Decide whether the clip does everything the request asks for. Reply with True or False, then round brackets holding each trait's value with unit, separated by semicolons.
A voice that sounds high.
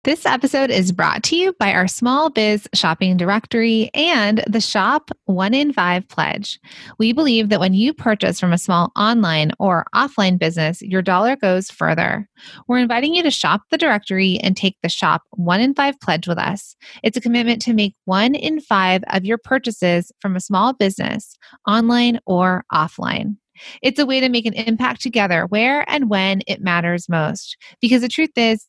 True (215 Hz)